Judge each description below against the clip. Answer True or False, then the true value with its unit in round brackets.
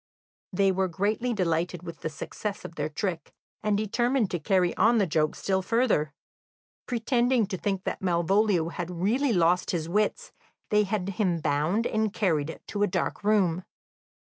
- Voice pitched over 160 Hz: True (190 Hz)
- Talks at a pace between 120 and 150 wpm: False (165 wpm)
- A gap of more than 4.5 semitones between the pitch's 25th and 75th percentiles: False (4.0 semitones)